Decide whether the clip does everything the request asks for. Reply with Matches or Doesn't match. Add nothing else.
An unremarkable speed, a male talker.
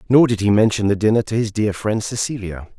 Doesn't match